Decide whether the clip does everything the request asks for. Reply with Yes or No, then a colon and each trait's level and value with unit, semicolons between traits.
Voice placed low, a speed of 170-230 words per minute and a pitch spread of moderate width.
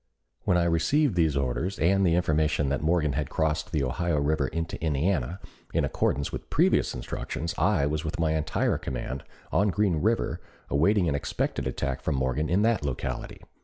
Yes: very low, 80 Hz; average, 175 wpm; average, 3.6 semitones